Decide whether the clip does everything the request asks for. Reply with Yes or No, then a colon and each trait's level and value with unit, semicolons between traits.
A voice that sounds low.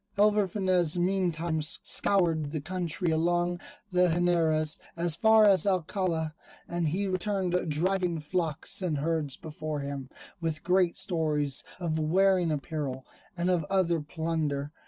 No: medium, 170 Hz